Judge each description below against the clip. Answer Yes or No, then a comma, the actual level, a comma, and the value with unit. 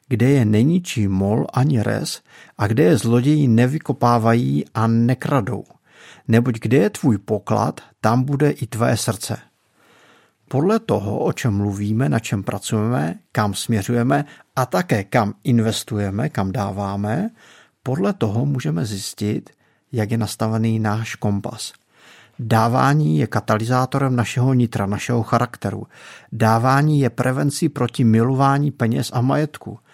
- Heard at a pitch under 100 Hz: No, low, 120 Hz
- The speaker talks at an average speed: Yes, average, 125 wpm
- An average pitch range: Yes, average, 3.7 semitones